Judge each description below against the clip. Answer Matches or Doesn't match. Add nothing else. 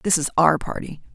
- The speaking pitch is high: Doesn't match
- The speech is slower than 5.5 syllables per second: Doesn't match